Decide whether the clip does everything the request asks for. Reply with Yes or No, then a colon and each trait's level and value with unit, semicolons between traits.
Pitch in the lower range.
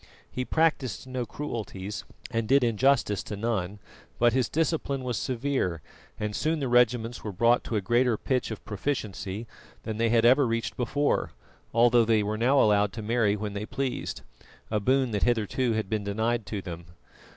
Yes: low, 115 Hz